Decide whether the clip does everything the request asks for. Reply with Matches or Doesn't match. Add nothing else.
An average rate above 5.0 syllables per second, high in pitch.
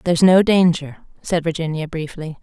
Doesn't match